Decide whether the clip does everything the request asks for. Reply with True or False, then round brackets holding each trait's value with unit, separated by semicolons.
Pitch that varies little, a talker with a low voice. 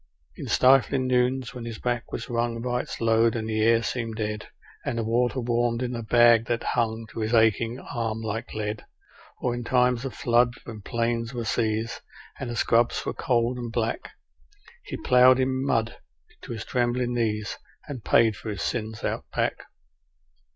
True (1.6 semitones; 115 Hz)